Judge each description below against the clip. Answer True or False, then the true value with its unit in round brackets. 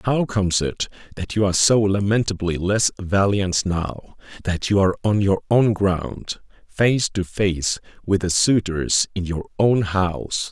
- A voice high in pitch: False (100 Hz)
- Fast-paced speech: False (160 wpm)